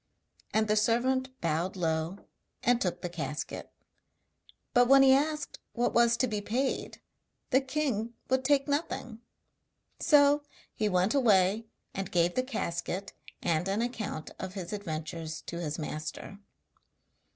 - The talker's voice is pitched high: Yes, high, 215 Hz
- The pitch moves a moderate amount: No, wide, 6.6 semitones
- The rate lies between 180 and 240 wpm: No, average, 140 wpm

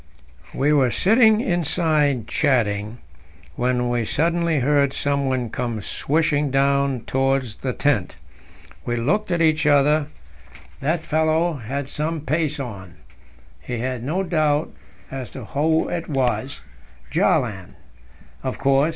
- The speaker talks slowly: Yes, slow, 125 wpm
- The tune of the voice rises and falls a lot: No, average, 3.9 semitones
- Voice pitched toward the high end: No, medium, 140 Hz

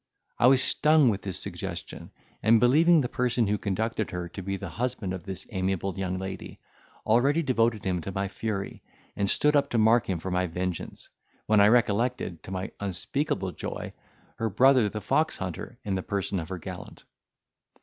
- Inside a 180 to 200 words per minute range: Yes, average, 185 wpm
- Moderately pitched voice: No, low, 100 Hz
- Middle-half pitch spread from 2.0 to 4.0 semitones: No, average, 4.4 semitones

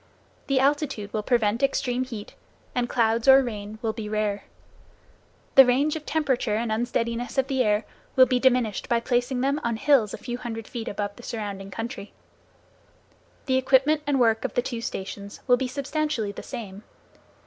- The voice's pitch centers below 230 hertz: No, high, 240 Hz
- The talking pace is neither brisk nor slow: Yes, average, 175 wpm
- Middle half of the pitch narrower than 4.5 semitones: Yes, average, 3.4 semitones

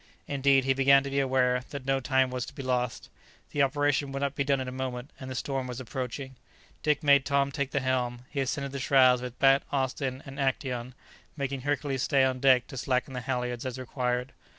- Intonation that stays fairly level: Yes, narrow, 1.5 semitones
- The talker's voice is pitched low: Yes, low, 130 Hz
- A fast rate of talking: Yes, fast, 220 wpm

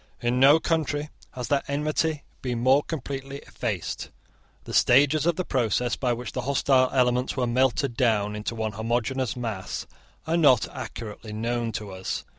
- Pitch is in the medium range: No, low, 125 Hz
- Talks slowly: No, average, 160 wpm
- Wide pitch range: No, average, 3.3 semitones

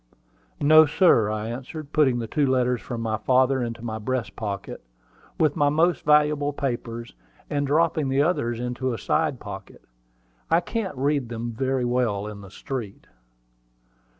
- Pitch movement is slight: No, average, 4.0 semitones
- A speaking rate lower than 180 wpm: Yes, average, 155 wpm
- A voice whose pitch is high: No, low, 130 Hz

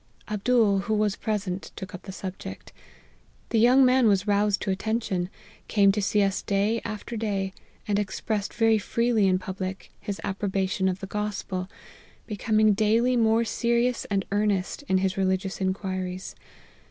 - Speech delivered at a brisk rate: No, average, 155 wpm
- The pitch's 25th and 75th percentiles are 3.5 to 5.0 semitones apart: No, narrow, 2.4 semitones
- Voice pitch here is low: No, high, 205 Hz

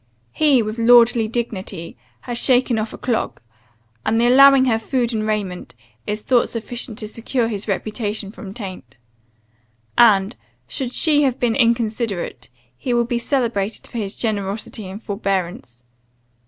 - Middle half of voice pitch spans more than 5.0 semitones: No, average, 2.9 semitones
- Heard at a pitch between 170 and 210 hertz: No, high, 225 Hz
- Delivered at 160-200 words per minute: No, average, 145 wpm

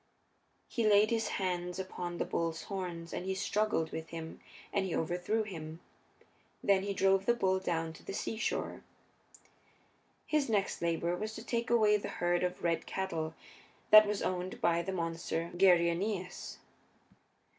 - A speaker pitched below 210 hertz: Yes, medium, 185 Hz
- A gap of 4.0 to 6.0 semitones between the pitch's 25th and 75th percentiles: No, average, 3.3 semitones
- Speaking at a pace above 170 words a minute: No, average, 155 wpm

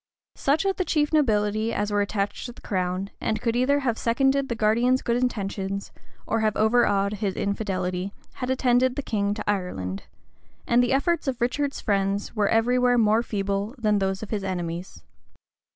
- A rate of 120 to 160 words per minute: No, average, 180 wpm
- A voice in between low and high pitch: No, high, 215 Hz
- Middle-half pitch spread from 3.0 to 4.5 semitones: Yes, average, 3.9 semitones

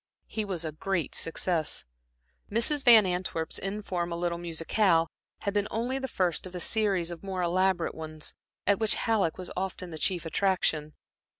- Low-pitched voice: No, medium, 185 Hz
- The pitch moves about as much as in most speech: Yes, average, 3.3 semitones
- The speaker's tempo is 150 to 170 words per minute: Yes, average, 165 wpm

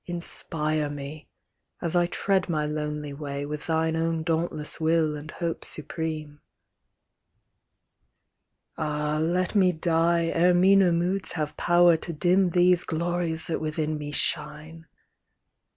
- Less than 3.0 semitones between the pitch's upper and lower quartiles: Yes, narrow, 2.4 semitones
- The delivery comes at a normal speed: No, slow, 125 wpm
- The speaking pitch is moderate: Yes, medium, 160 Hz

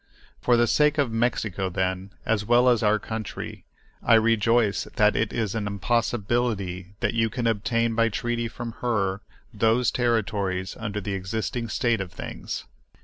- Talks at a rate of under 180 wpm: Yes, average, 160 wpm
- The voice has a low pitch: Yes, low, 110 Hz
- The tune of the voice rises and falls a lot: No, average, 2.7 semitones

